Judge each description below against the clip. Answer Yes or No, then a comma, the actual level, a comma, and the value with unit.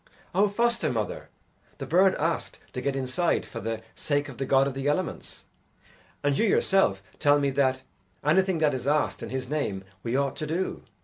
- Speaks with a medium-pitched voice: Yes, medium, 145 Hz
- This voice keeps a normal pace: Yes, average, 190 wpm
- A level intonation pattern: No, average, 4.2 semitones